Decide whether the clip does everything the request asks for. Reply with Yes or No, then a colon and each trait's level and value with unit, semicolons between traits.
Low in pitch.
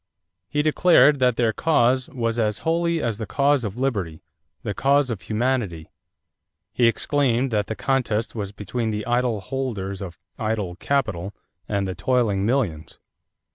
Yes: low, 115 Hz